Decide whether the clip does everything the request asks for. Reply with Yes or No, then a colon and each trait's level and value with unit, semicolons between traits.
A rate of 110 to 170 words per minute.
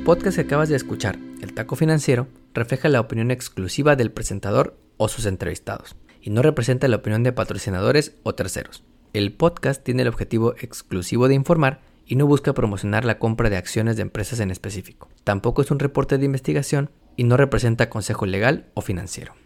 No: average, 180 wpm